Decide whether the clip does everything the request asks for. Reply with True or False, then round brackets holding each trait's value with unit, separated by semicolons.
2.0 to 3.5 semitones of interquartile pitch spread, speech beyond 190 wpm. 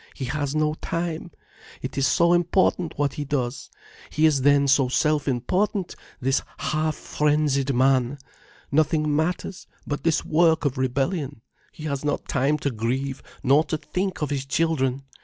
False (2.7 semitones; 160 wpm)